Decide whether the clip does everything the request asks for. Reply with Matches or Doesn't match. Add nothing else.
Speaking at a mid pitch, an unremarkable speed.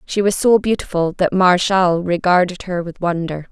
Matches